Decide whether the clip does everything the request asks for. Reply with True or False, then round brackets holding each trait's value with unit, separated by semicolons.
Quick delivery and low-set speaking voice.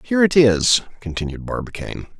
False (135 wpm; 120 Hz)